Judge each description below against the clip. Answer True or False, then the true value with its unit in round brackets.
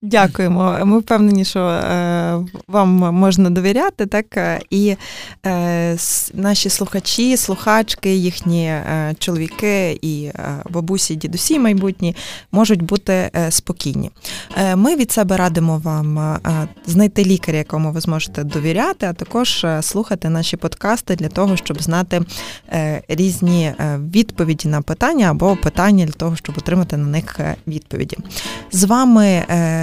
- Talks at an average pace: True (115 wpm)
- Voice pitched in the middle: True (180 Hz)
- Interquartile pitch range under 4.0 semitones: True (3.6 semitones)